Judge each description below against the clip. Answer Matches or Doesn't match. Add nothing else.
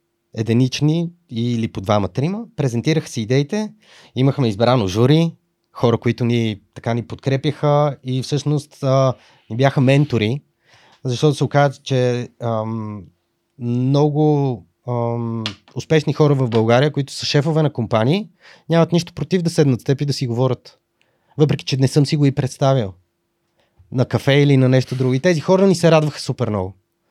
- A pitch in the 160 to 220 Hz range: Doesn't match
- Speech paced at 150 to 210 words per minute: Matches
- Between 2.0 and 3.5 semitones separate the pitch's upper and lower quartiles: Doesn't match